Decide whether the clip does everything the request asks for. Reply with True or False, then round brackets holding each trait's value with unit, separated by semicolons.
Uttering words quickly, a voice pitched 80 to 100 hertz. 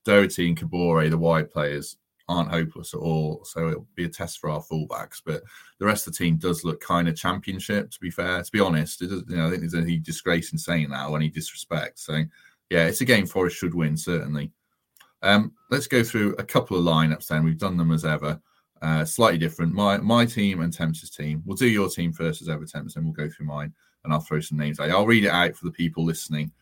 True (240 wpm; 85 Hz)